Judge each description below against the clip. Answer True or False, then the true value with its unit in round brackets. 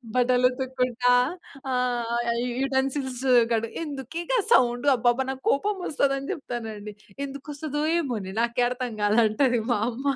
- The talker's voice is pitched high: True (250 Hz)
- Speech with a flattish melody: True (2.3 semitones)